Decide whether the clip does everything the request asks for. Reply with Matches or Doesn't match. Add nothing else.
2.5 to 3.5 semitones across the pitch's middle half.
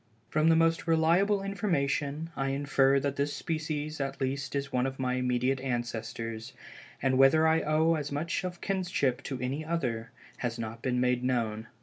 Doesn't match